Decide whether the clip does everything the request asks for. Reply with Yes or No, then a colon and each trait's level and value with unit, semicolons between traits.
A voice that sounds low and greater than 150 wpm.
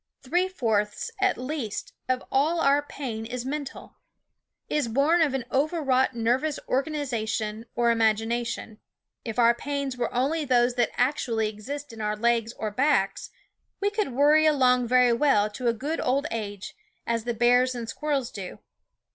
No: very high, 250 Hz; average, 165 wpm